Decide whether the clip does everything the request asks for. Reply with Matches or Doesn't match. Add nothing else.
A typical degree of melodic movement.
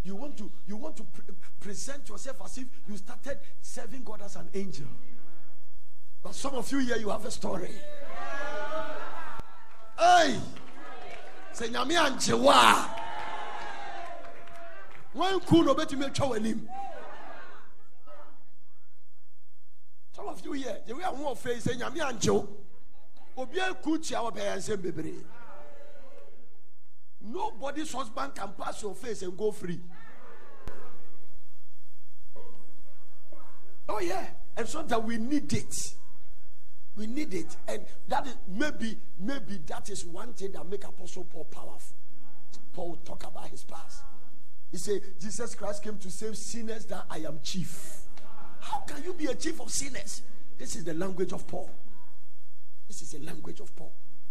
Doesn't match